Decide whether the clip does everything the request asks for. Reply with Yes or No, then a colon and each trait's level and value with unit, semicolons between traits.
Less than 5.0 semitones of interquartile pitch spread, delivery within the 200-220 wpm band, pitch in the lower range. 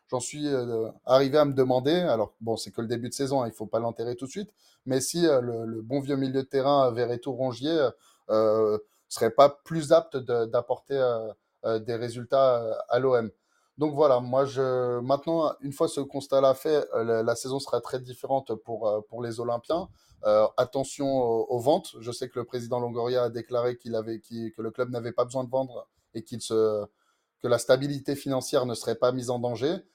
Yes: average, 2.9 semitones; average, 210 wpm; low, 125 Hz